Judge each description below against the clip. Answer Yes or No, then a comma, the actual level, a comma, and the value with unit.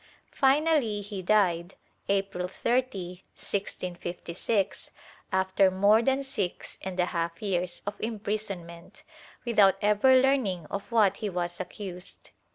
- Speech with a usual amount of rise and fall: Yes, average, 3.2 semitones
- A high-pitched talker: Yes, high, 195 Hz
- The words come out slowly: Yes, slow, 115 wpm